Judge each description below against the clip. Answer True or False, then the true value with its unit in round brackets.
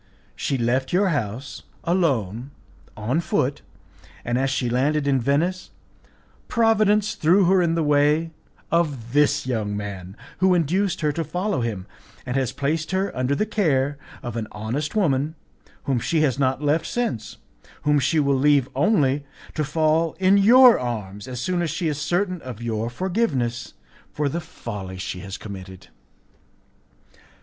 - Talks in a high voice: False (145 Hz)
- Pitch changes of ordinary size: False (5.9 semitones)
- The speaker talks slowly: False (155 wpm)